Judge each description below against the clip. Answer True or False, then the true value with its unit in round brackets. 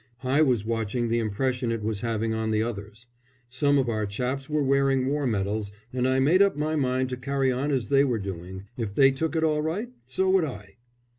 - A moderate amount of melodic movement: True (4.1 semitones)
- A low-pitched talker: True (130 Hz)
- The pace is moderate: False (220 wpm)